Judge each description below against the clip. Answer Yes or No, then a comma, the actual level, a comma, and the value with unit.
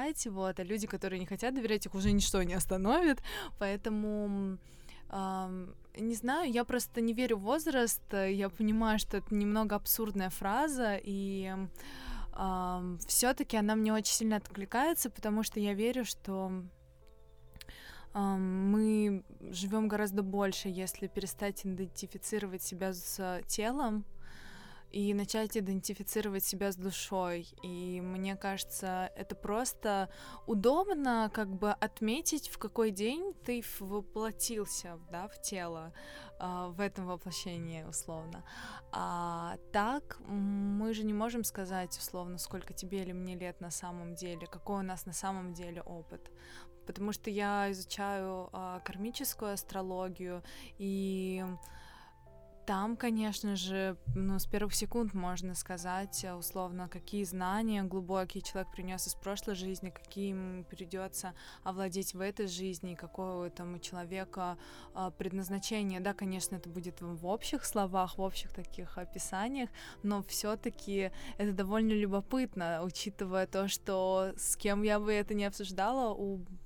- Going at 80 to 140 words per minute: Yes, average, 130 wpm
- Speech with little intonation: Yes, narrow, 2.3 semitones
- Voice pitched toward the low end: No, high, 195 Hz